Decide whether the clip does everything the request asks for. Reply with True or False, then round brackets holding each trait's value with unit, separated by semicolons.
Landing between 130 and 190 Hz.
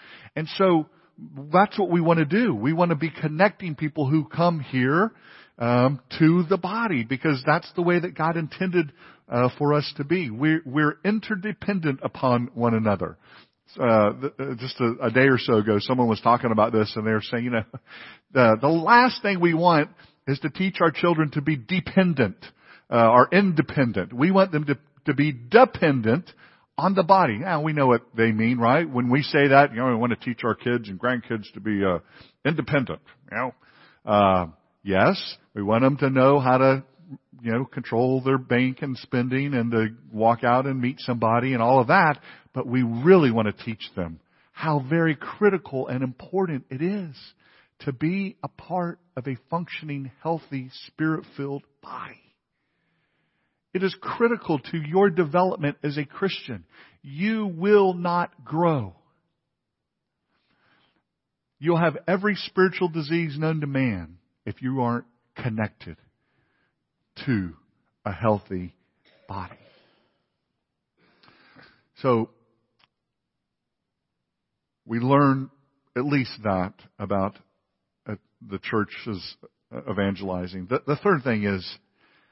True (140 Hz)